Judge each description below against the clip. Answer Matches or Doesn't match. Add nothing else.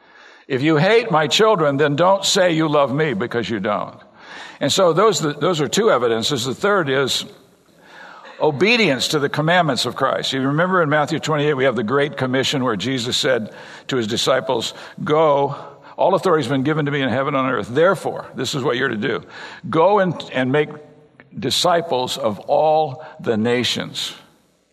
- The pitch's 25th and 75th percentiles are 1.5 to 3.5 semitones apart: Matches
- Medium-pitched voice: Matches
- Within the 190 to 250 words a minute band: Doesn't match